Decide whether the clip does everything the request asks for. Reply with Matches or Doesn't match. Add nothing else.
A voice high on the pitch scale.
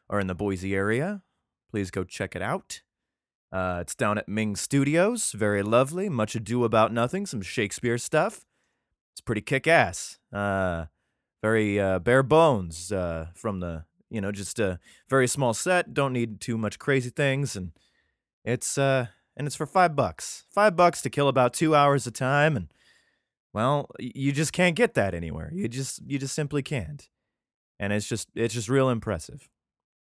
Doesn't match